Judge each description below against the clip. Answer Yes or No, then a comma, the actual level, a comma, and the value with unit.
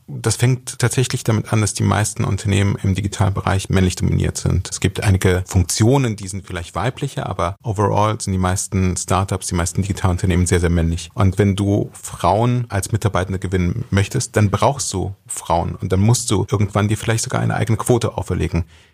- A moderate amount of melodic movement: Yes, average, 3.3 semitones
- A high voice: No, low, 100 Hz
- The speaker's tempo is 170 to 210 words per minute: Yes, average, 185 wpm